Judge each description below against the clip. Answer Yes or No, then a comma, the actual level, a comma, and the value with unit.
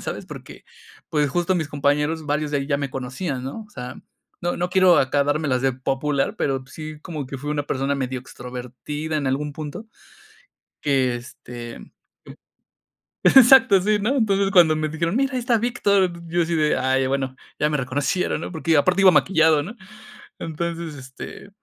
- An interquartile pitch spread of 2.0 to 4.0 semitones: No, average, 4.6 semitones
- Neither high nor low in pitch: Yes, medium, 150 Hz